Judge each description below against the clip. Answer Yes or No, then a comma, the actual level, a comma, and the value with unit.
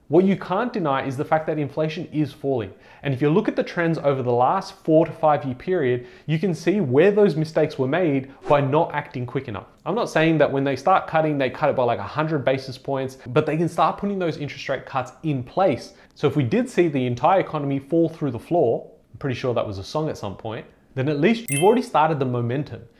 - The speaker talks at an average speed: No, fast, 250 wpm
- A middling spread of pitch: Yes, average, 3.6 semitones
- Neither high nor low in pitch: Yes, medium, 145 Hz